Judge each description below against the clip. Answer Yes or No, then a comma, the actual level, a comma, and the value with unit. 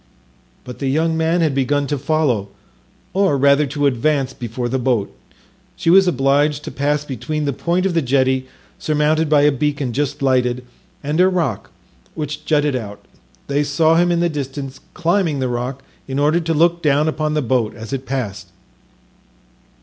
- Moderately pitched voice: Yes, medium, 145 Hz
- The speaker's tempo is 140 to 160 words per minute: No, average, 175 wpm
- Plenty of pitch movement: No, average, 3.1 semitones